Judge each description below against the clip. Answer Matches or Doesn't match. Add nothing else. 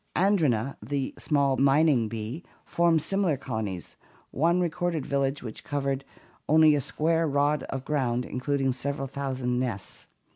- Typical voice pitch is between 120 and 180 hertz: Matches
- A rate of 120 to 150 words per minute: Matches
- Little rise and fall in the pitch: Doesn't match